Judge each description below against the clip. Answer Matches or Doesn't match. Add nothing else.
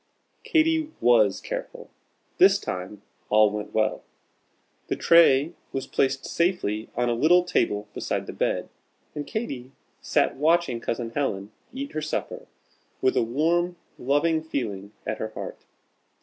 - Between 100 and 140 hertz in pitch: Matches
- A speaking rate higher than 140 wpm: Doesn't match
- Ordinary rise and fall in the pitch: Doesn't match